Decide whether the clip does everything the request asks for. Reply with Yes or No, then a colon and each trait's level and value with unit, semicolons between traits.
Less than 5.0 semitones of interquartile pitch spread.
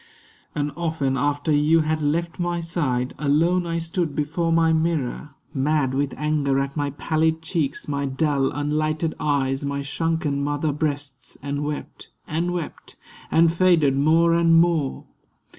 Yes: narrow, 2.6 semitones